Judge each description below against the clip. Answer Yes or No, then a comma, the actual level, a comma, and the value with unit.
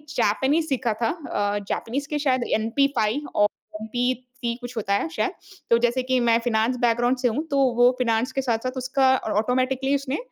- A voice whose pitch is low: No, very high, 250 Hz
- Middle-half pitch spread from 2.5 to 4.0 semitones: Yes, average, 2.8 semitones